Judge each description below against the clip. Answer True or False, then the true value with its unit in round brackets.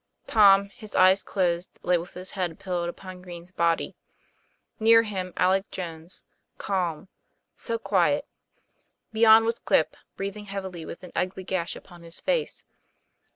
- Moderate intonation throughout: False (2.3 semitones)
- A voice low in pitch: False (185 Hz)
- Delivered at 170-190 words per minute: False (145 wpm)